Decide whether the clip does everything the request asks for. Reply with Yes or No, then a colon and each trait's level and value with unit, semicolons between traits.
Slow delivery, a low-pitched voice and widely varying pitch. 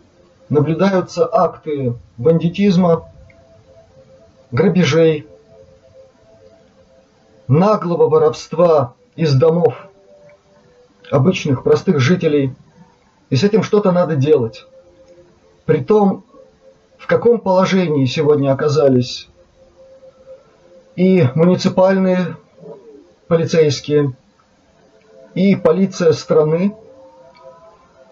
No: slow, 65 wpm; medium, 160 Hz; wide, 6.0 semitones